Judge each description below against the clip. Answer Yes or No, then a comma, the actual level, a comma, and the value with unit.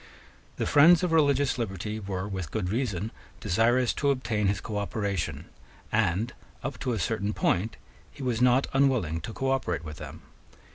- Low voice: Yes, low, 110 Hz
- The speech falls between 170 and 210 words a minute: No, average, 155 wpm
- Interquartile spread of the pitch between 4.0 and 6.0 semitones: Yes, average, 5.2 semitones